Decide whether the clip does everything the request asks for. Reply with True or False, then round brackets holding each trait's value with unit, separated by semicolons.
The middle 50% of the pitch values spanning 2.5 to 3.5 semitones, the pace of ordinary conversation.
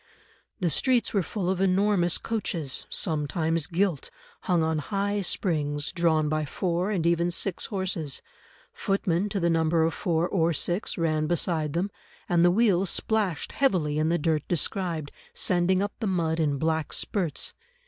True (3.2 semitones; 160 wpm)